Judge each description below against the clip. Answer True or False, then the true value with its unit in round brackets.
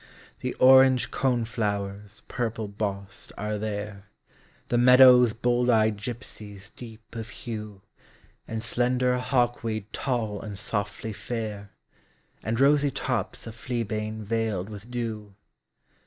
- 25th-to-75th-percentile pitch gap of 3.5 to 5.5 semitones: False (2.8 semitones)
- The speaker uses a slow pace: True (115 wpm)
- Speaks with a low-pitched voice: True (110 Hz)